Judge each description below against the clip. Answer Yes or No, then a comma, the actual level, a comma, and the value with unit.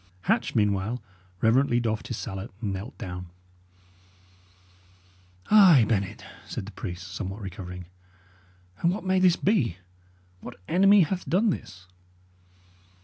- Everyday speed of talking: No, slow, 120 wpm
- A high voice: No, low, 110 Hz